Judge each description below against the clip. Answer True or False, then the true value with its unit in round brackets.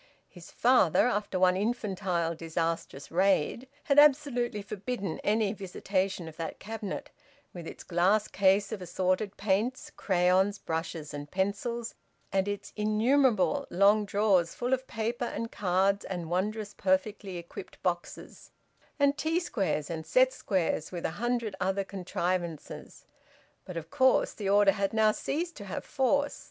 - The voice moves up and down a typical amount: True (3.9 semitones)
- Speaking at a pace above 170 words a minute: False (145 wpm)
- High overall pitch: True (200 Hz)